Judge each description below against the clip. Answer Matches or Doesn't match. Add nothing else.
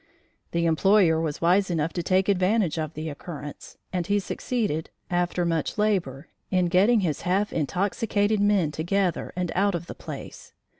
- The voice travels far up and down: Doesn't match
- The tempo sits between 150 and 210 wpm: Matches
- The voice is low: Doesn't match